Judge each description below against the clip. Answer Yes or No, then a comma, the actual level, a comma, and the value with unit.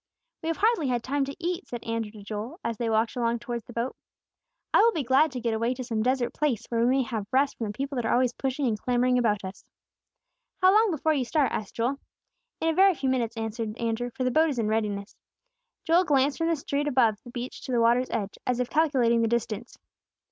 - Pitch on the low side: No, high, 245 Hz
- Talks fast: Yes, fast, 240 wpm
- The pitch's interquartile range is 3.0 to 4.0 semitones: Yes, average, 3.6 semitones